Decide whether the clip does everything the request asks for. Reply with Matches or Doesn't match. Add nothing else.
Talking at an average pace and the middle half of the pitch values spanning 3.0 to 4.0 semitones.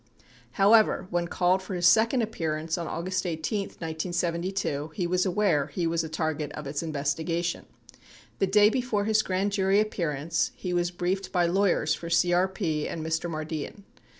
Matches